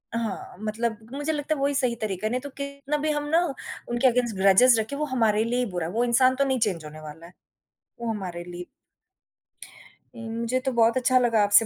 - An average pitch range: Yes, average, 4.2 semitones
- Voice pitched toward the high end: Yes, high, 235 Hz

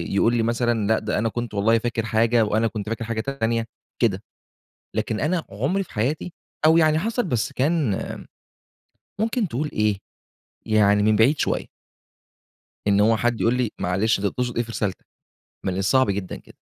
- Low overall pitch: Yes, low, 115 Hz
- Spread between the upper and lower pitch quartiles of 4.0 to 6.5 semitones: No, average, 3.5 semitones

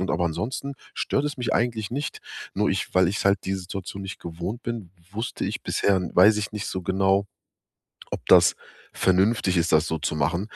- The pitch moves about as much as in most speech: Yes, average, 3.4 semitones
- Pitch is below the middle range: Yes, very low, 95 Hz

